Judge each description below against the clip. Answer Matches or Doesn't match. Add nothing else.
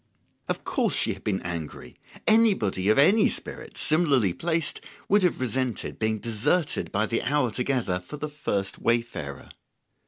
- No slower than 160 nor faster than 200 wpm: Doesn't match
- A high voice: Doesn't match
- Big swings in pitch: Matches